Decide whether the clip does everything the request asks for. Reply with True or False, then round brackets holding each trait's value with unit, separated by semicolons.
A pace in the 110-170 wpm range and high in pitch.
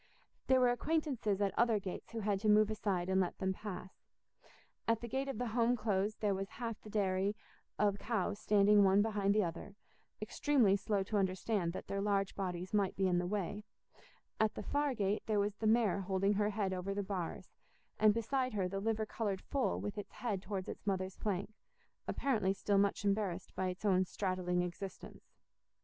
False (195 wpm; 205 Hz)